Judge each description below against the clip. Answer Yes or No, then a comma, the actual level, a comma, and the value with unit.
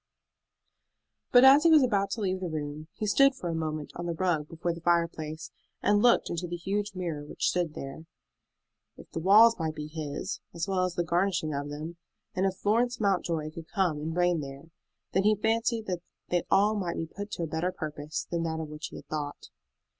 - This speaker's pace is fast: Yes, fast, 215 wpm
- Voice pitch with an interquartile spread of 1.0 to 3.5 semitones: No, average, 4.0 semitones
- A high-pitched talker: No, medium, 175 Hz